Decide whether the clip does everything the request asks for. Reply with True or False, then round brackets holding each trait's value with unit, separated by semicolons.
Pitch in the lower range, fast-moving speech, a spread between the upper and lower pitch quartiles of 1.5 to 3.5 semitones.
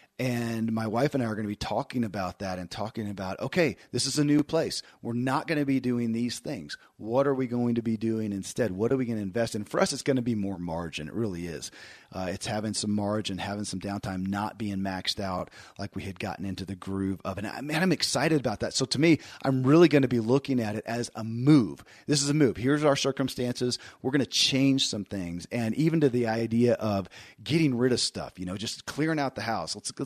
False (115 Hz; 260 wpm; 5.1 semitones)